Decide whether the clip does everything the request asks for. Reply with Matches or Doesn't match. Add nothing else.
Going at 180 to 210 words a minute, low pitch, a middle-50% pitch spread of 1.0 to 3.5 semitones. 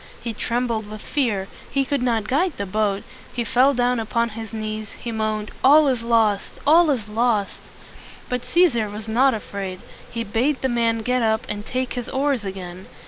Doesn't match